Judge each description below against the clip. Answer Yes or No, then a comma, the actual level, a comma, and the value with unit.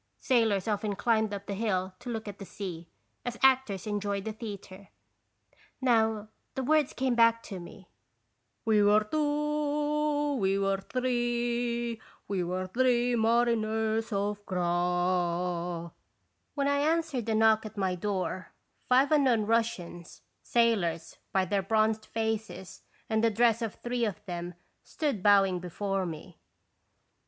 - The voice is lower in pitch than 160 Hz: No, high, 220 Hz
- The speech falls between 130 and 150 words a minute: Yes, slow, 135 wpm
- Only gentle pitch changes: No, average, 4.0 semitones